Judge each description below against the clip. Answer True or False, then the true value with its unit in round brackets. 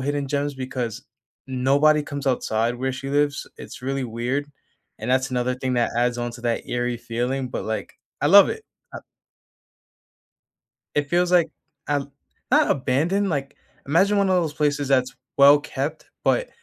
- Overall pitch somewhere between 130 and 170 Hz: True (135 Hz)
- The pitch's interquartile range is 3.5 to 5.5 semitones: False (2.7 semitones)